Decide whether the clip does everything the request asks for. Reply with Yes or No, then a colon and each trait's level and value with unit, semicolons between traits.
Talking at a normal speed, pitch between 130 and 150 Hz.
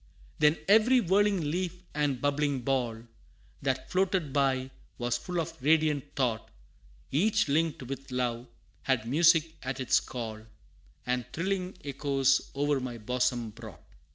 No: slow, 130 wpm; medium, 140 Hz